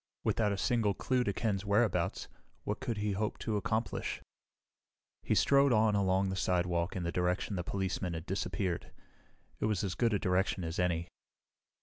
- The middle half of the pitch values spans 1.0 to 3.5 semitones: Yes, average, 3.0 semitones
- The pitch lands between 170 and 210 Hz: No, low, 100 Hz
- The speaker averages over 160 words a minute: Yes, average, 170 wpm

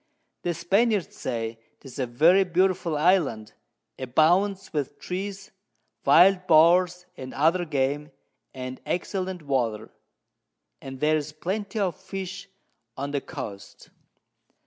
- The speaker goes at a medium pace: No, slow, 110 wpm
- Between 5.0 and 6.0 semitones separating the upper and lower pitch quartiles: Yes, wide, 5.6 semitones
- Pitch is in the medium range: Yes, medium, 165 Hz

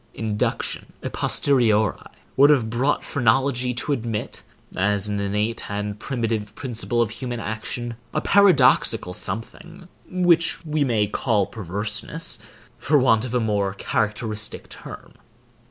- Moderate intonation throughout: Yes, average, 4.3 semitones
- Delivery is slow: Yes, slow, 125 wpm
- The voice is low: Yes, low, 115 Hz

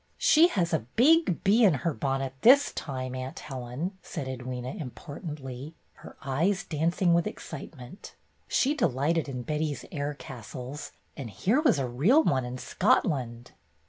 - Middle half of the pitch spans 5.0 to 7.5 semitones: Yes, wide, 5.6 semitones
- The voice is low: No, medium, 145 Hz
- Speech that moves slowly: No, average, 145 wpm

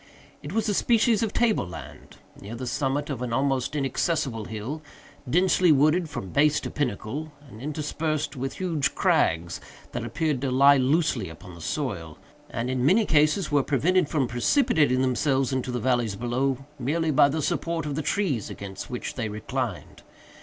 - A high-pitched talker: No, medium, 140 Hz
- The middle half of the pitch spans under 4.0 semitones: No, average, 4.3 semitones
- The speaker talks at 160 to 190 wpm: Yes, average, 170 wpm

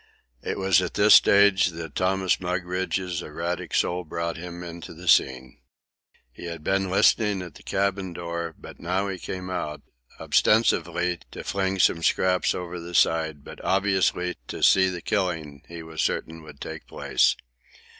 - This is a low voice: Yes, very low, 90 Hz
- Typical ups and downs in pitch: No, narrow, 2.3 semitones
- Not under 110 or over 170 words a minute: Yes, average, 160 wpm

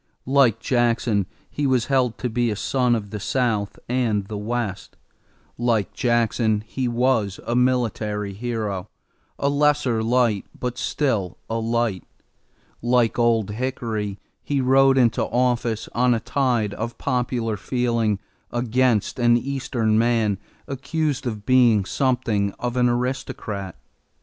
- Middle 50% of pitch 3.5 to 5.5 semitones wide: No, average, 2.7 semitones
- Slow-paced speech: Yes, slow, 130 wpm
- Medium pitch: No, low, 120 Hz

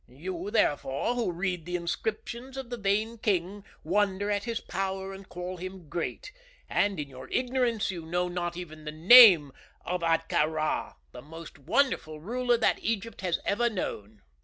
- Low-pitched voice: No, medium, 185 Hz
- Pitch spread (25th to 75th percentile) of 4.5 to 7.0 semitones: Yes, average, 5.1 semitones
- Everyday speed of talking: Yes, average, 165 wpm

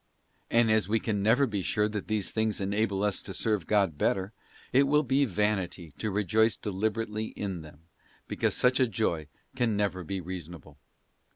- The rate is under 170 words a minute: No, average, 175 wpm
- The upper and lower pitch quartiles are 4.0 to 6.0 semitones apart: No, average, 2.8 semitones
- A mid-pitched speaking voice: No, low, 105 Hz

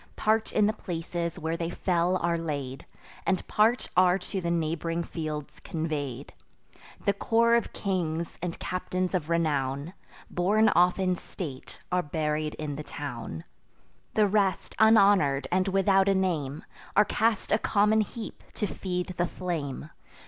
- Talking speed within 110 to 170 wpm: Yes, average, 150 wpm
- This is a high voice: No, medium, 175 Hz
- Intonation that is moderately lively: Yes, average, 4.0 semitones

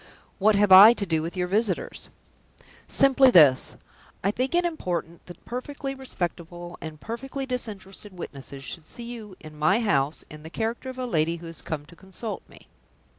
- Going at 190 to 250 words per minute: No, average, 180 wpm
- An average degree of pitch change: No, wide, 6.4 semitones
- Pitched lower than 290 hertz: Yes, high, 190 Hz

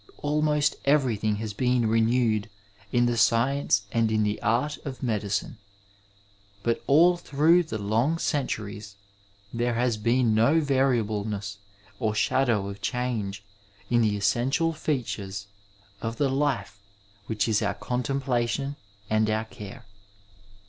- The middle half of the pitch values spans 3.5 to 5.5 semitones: Yes, average, 4.2 semitones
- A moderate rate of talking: No, slow, 125 wpm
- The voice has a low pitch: Yes, low, 115 Hz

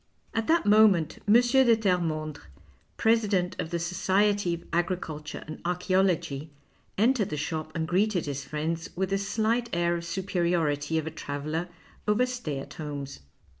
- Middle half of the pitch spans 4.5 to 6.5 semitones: Yes, average, 4.8 semitones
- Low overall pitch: No, medium, 175 Hz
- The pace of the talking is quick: No, average, 150 wpm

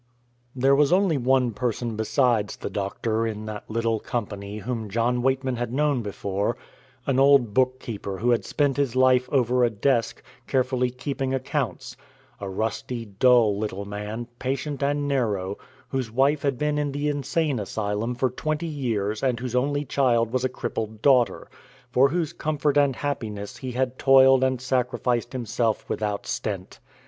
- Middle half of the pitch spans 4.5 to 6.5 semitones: No, average, 3.5 semitones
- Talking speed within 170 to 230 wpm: No, average, 160 wpm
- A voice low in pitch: Yes, low, 125 Hz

